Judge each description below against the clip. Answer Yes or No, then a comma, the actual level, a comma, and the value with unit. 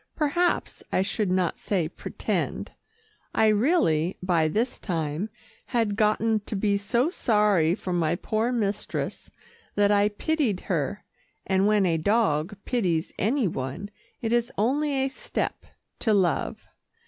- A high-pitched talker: Yes, high, 205 Hz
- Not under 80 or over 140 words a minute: Yes, slow, 135 wpm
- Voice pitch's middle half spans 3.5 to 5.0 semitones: Yes, average, 4.3 semitones